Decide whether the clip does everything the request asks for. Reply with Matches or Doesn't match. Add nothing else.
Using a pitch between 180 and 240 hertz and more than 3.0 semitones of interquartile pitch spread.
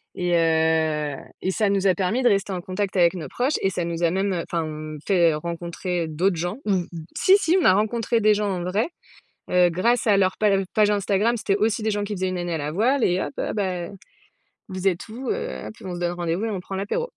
Matches